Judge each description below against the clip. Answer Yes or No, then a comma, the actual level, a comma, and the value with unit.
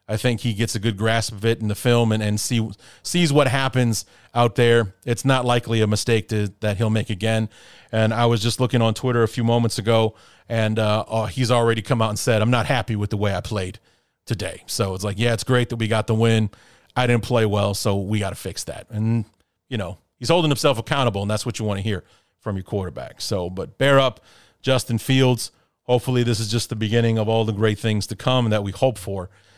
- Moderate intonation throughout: No, narrow, 2.2 semitones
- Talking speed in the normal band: No, fast, 245 wpm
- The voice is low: Yes, low, 115 Hz